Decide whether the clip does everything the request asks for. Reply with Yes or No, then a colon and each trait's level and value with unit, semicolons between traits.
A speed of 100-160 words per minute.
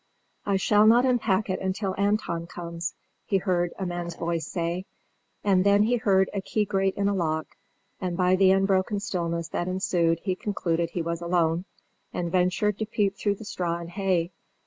No: average, 185 wpm